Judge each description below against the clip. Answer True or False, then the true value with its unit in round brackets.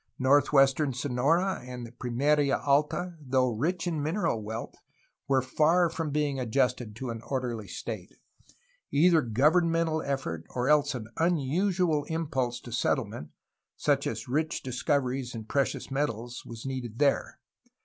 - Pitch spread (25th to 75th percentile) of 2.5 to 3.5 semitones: False (4.0 semitones)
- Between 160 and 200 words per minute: False (135 wpm)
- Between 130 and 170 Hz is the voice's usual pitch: True (135 Hz)